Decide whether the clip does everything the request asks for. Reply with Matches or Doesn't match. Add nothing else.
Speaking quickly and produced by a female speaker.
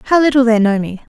Matches